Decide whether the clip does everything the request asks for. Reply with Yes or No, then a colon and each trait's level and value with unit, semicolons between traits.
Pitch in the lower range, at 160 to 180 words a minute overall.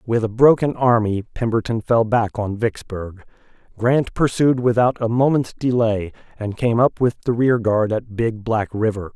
Yes: low, 115 Hz; average, 170 wpm